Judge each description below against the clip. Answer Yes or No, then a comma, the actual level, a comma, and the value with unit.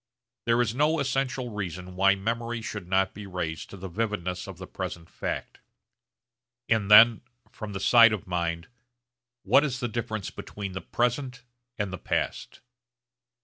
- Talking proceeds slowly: No, average, 155 wpm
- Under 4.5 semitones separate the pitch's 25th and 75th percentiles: Yes, average, 4.1 semitones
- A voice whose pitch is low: Yes, low, 105 Hz